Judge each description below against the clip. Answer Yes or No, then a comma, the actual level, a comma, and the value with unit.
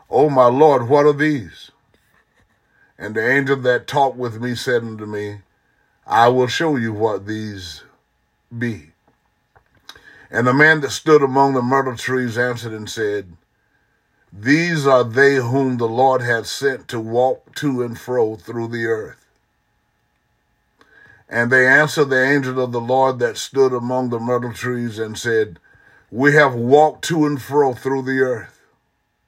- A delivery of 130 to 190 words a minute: Yes, average, 155 wpm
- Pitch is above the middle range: No, low, 125 Hz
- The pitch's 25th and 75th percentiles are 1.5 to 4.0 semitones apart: Yes, average, 2.9 semitones